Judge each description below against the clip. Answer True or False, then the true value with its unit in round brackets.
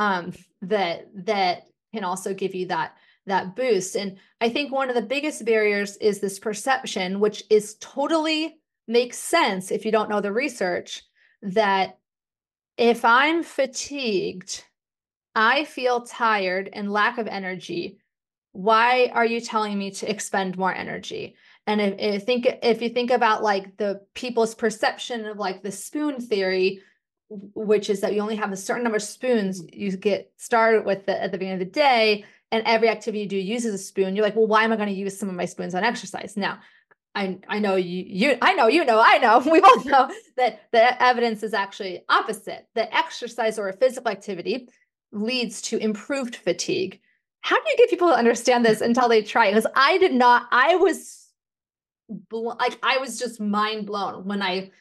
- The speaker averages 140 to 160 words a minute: False (185 wpm)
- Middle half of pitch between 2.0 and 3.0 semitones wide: False (3.7 semitones)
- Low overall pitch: False (220 Hz)